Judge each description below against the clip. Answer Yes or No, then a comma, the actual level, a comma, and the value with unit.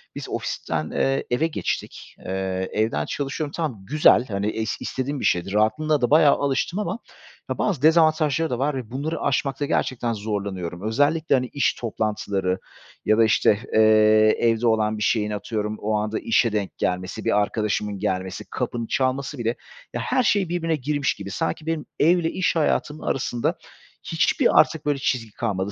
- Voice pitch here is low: Yes, low, 120 Hz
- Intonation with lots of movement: Yes, wide, 5.9 semitones